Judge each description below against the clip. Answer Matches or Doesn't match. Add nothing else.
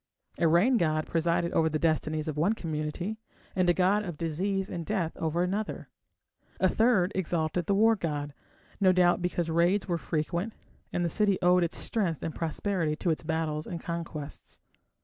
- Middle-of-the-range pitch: Matches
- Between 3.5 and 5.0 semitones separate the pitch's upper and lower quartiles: Doesn't match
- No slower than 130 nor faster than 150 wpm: Doesn't match